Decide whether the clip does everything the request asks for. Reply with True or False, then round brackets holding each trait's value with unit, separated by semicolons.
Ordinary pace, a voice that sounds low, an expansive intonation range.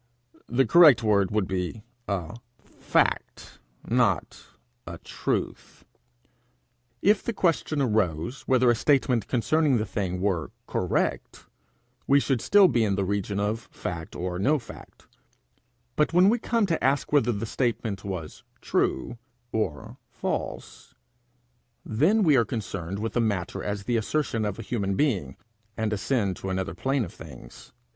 True (145 wpm; 110 Hz; 5.7 semitones)